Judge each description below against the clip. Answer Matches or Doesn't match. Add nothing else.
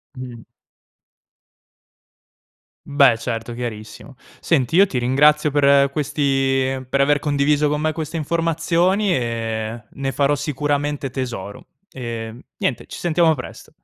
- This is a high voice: Doesn't match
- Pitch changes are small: Doesn't match